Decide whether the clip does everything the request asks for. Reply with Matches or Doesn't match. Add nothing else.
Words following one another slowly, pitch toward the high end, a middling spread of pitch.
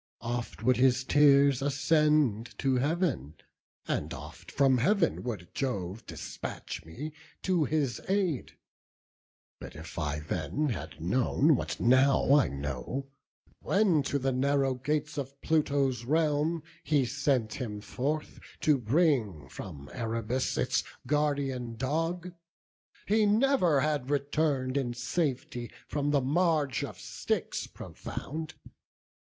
Doesn't match